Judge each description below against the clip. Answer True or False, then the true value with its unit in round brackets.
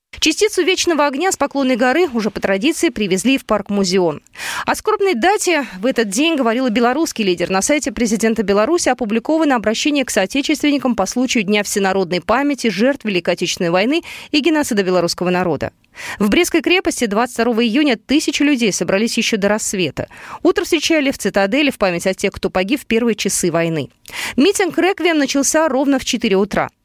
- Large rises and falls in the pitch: True (6.9 semitones)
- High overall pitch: True (245 Hz)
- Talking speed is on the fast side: True (170 wpm)